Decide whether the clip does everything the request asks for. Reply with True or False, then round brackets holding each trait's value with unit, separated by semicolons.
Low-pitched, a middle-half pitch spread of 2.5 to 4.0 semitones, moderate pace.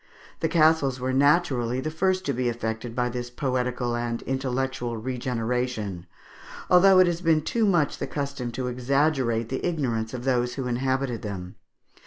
True (130 Hz; 3.1 semitones; 160 wpm)